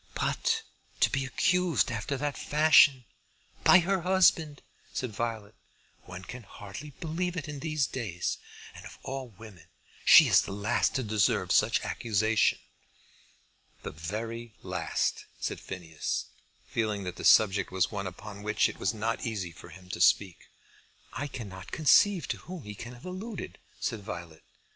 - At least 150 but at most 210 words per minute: Yes, average, 155 wpm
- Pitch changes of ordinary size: No, wide, 6.7 semitones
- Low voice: Yes, low, 115 Hz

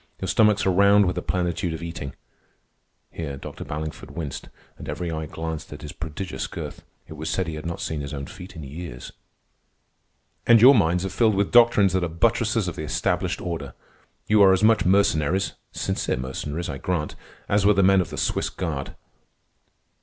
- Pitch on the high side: No, very low, 85 Hz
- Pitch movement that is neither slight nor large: Yes, average, 4.1 semitones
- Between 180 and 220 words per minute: Yes, average, 190 wpm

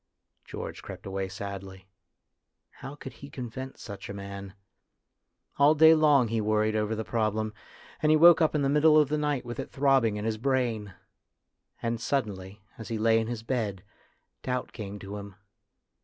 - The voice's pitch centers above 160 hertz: No, low, 115 Hz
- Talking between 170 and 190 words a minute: Yes, average, 175 wpm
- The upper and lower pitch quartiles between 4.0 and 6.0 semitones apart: Yes, average, 4.8 semitones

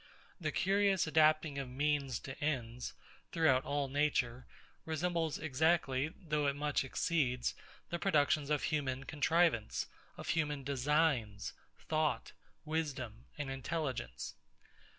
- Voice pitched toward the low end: No, medium, 145 Hz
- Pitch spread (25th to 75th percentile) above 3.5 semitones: No, average, 3.2 semitones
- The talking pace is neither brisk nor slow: No, slow, 110 wpm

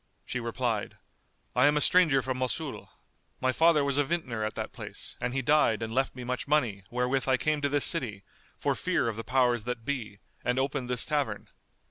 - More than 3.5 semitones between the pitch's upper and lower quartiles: No, average, 3.2 semitones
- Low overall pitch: Yes, low, 130 Hz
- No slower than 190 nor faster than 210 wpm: Yes, fast, 205 wpm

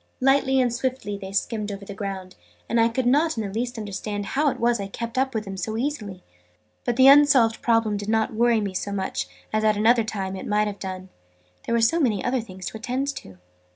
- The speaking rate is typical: No, fast, 230 wpm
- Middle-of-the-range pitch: No, high, 220 Hz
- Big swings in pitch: No, average, 3.6 semitones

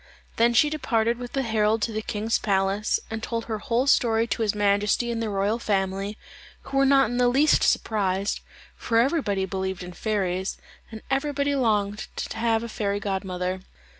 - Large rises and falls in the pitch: No, average, 3.0 semitones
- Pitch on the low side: No, high, 220 Hz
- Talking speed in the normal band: Yes, average, 180 wpm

